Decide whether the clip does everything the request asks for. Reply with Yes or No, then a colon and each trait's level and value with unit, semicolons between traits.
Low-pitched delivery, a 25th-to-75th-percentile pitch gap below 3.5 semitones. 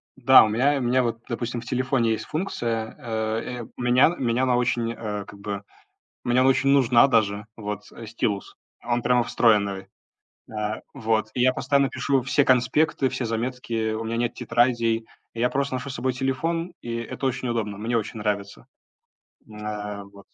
Yes: low, 120 Hz; average, 2.8 semitones